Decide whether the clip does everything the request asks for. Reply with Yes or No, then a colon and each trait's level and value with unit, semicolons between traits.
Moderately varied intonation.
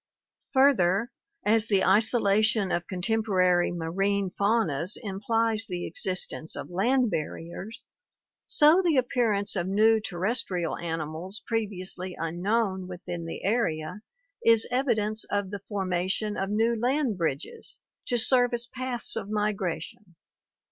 Yes: average, 4.0 semitones